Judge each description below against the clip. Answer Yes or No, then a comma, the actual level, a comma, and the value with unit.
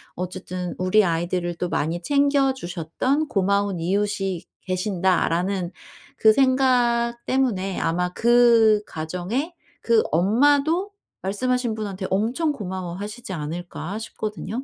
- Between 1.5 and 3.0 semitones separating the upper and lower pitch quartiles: No, average, 5.2 semitones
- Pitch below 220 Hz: Yes, high, 200 Hz